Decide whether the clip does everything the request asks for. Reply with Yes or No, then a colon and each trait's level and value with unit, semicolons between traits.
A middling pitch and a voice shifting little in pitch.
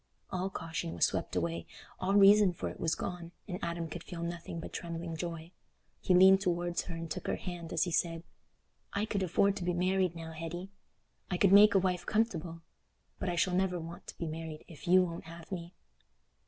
Yes: medium, 175 Hz; narrow, 2.0 semitones